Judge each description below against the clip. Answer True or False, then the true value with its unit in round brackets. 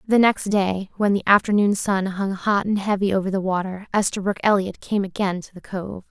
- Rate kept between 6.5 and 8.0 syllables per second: False (5.2 syllables/s)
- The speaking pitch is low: False (195 Hz)